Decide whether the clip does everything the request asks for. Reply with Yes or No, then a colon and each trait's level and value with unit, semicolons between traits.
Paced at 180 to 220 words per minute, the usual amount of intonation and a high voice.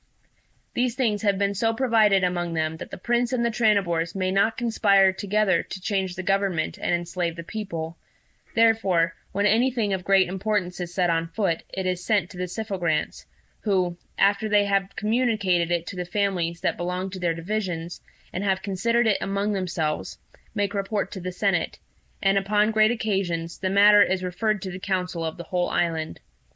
Yes: average, 190 wpm; average, 3.0 semitones; high, 195 Hz